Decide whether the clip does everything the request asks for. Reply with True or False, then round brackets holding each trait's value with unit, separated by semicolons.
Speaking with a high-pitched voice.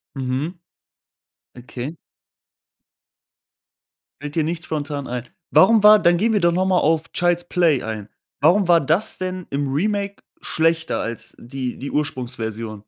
False (160 Hz)